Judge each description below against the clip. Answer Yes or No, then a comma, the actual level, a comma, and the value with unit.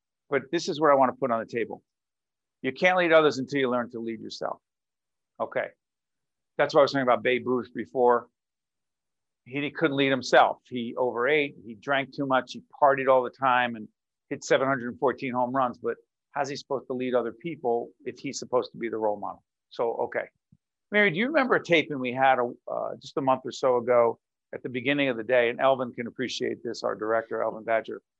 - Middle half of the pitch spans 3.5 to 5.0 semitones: No, average, 2.9 semitones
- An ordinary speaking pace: No, fast, 215 wpm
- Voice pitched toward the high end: No, low, 130 Hz